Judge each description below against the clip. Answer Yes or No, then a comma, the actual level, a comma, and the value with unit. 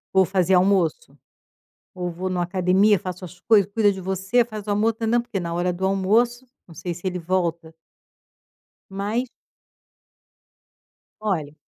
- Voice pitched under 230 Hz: Yes, high, 190 Hz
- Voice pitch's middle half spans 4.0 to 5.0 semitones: No, average, 2.8 semitones